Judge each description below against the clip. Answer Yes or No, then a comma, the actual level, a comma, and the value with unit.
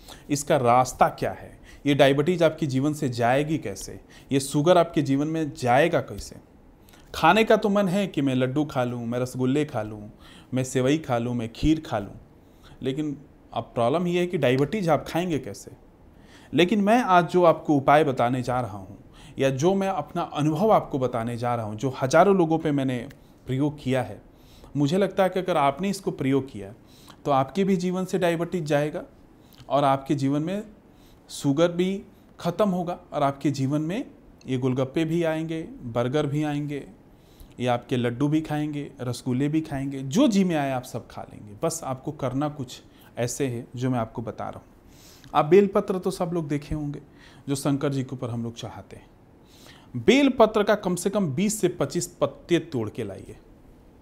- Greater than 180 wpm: Yes, fast, 190 wpm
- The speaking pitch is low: No, medium, 145 Hz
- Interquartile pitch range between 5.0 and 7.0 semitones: Yes, average, 5.3 semitones